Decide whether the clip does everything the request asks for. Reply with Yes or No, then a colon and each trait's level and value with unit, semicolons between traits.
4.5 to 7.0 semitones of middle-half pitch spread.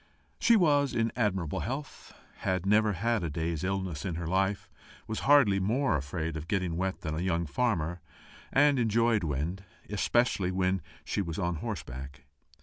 Yes: wide, 5.4 semitones